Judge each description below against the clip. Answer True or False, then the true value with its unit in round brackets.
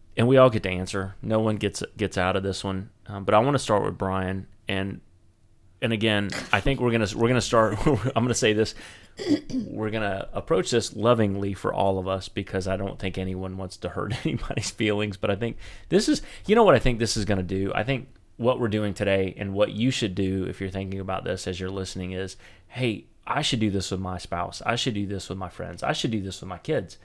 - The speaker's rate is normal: False (255 wpm)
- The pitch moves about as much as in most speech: True (3.3 semitones)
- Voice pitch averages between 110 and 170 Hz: False (100 Hz)